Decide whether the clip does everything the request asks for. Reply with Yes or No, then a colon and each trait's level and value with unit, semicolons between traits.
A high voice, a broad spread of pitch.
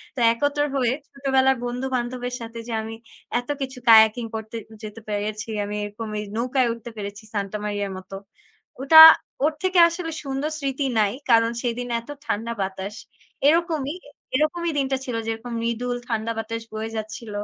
No: high, 235 Hz; average, 3.5 semitones